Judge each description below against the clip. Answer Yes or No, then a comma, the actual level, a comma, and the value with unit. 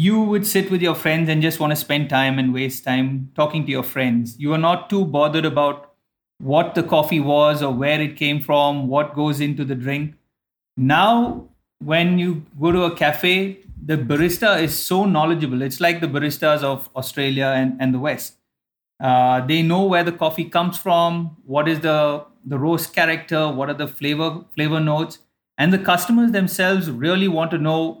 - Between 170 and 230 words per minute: Yes, average, 190 wpm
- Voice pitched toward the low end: No, medium, 155 Hz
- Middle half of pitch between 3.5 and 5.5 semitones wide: No, average, 2.9 semitones